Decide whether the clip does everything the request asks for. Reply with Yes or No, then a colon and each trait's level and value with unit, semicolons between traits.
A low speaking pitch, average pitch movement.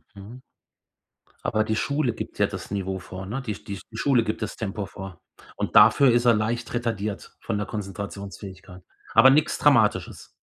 Yes: low, 105 Hz; average, 3.4 semitones